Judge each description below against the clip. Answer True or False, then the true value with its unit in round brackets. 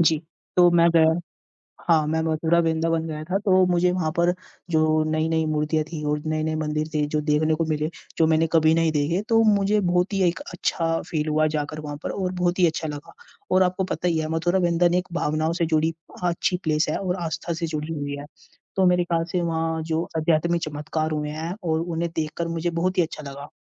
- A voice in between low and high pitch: True (160 Hz)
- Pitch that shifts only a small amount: True (1.9 semitones)